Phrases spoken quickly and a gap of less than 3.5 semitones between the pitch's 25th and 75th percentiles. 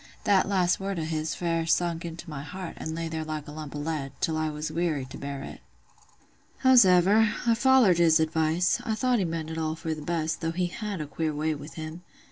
Yes: fast, 230 wpm; narrow, 2.6 semitones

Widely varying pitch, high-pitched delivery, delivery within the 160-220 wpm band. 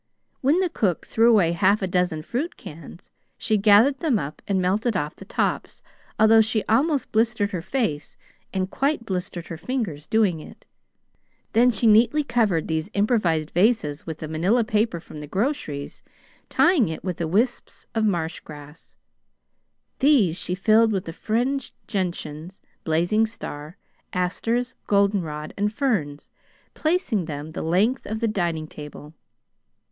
No: wide, 5.9 semitones; high, 200 Hz; average, 145 wpm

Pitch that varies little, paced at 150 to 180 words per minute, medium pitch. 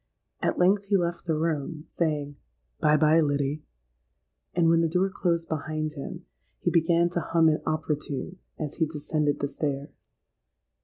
Yes: narrow, 2.2 semitones; average, 160 wpm; medium, 155 Hz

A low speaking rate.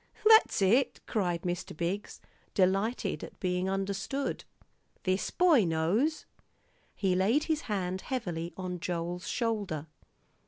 Yes: slow, 115 wpm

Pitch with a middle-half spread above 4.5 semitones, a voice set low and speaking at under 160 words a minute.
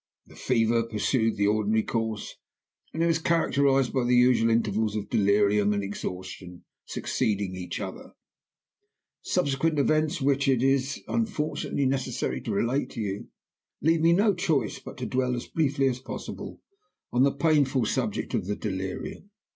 Yes: average, 5.1 semitones; low, 125 Hz; average, 150 wpm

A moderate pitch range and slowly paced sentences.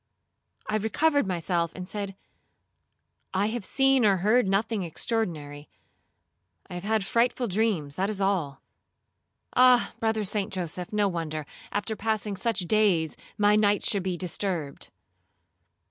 Yes: average, 3.7 semitones; slow, 130 wpm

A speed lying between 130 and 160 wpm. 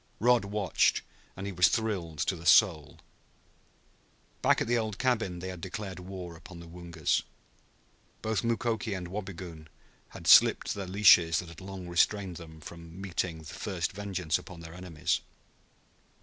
Yes: average, 150 wpm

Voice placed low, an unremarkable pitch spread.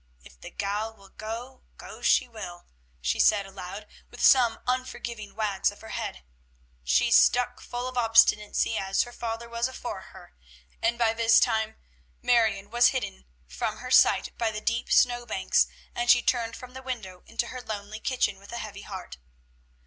No: high, 225 Hz; average, 3.1 semitones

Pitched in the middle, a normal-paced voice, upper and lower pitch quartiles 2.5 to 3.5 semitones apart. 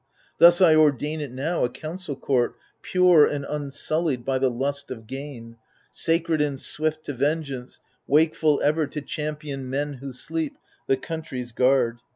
Yes: medium, 145 Hz; average, 155 wpm; average, 3.0 semitones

